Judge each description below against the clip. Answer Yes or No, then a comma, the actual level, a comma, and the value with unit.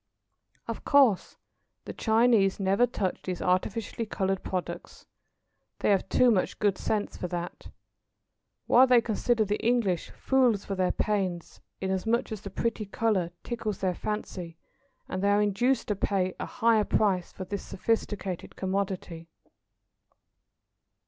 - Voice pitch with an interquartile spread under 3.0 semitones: No, average, 3.3 semitones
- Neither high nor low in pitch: No, high, 200 Hz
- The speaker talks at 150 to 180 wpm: No, slow, 135 wpm